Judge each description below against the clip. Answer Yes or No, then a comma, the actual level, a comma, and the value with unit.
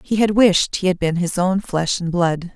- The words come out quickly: Yes, fast, 260 wpm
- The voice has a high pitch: No, medium, 180 Hz